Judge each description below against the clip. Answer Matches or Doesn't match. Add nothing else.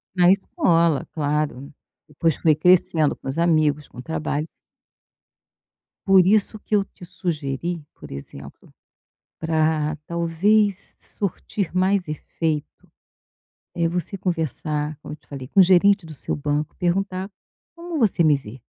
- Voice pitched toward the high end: Doesn't match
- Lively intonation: Doesn't match